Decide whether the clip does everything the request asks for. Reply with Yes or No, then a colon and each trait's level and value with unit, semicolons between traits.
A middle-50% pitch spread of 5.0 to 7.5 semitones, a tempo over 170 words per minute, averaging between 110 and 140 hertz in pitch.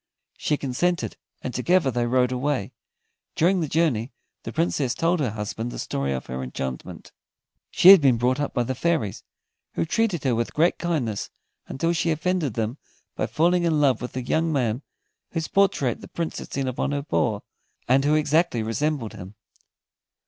Yes: wide, 5.6 semitones; average, 180 wpm; low, 135 Hz